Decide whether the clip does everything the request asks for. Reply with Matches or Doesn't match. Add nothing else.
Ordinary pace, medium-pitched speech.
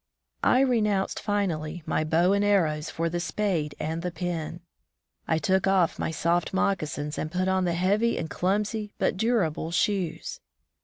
Matches